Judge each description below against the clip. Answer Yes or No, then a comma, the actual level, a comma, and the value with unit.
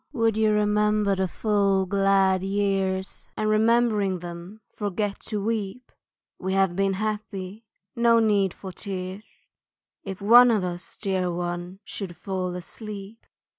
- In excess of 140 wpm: No, slow, 135 wpm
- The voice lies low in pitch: No, high, 195 Hz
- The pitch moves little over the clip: Yes, narrow, 2.2 semitones